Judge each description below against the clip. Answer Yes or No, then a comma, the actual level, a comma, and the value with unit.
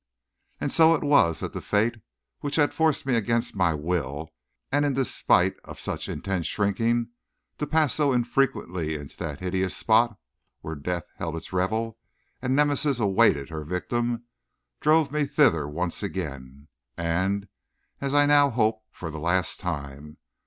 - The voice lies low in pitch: Yes, low, 105 Hz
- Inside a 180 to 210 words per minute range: No, average, 155 wpm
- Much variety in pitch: Yes, wide, 8.6 semitones